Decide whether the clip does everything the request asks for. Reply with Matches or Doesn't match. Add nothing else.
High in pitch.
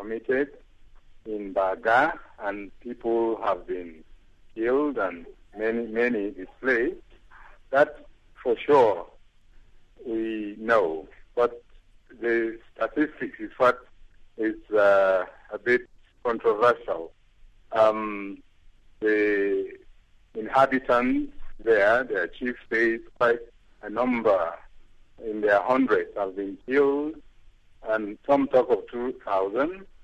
Doesn't match